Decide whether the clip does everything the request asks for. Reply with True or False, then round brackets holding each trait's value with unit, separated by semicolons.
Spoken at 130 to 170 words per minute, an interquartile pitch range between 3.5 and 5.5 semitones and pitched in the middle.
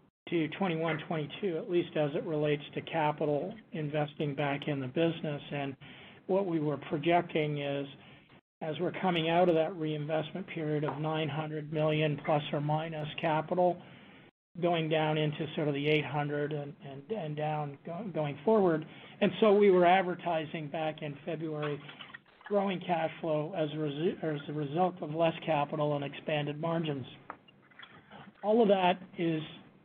False (155 wpm; 2.4 semitones; 155 Hz)